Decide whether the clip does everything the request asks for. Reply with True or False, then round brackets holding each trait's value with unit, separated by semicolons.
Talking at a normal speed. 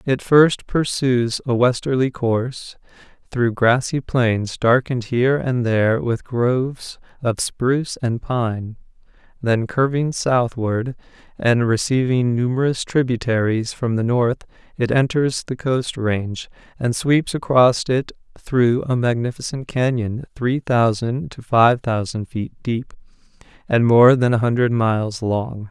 False (130 wpm)